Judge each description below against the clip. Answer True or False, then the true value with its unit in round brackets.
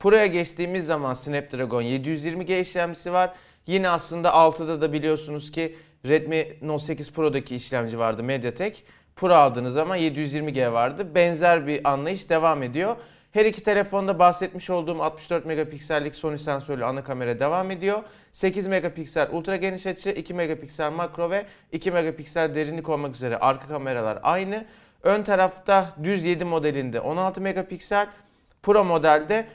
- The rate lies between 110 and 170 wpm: True (140 wpm)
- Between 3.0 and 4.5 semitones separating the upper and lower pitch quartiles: True (3.9 semitones)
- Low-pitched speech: False (165 Hz)